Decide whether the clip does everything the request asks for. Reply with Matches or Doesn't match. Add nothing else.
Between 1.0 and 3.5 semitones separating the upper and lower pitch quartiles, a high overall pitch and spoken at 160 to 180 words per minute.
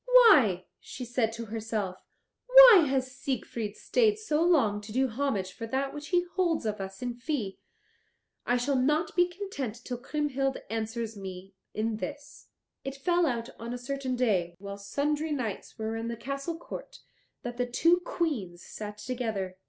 Doesn't match